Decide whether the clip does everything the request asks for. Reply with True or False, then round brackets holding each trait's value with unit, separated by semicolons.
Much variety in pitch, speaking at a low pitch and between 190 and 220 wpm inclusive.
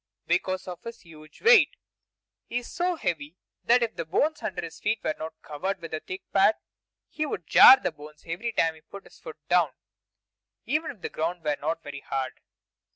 False (6.8 semitones; 175 Hz; 200 wpm)